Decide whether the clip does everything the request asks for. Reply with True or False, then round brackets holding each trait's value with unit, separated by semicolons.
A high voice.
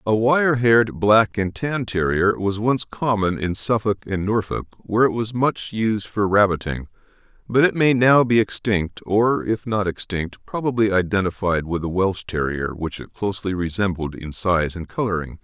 False (100 Hz)